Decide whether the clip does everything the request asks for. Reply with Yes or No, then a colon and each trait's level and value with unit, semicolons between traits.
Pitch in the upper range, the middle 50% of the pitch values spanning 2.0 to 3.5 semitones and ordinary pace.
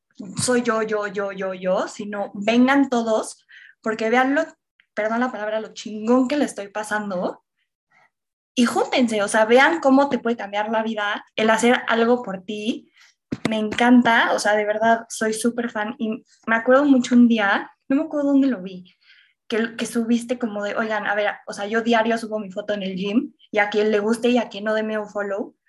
No: high, 225 Hz; average, 2.8 semitones; fast, 205 wpm